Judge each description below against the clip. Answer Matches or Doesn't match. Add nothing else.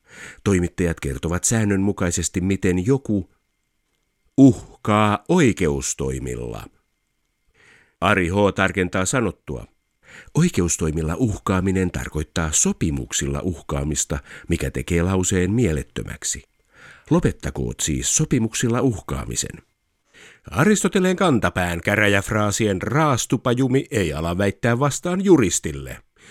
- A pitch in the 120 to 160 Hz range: Doesn't match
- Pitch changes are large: Matches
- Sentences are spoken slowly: Matches